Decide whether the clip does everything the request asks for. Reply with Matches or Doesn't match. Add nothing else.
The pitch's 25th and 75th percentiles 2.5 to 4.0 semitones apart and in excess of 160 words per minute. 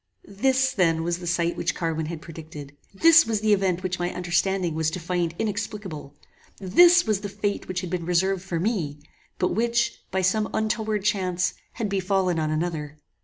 Matches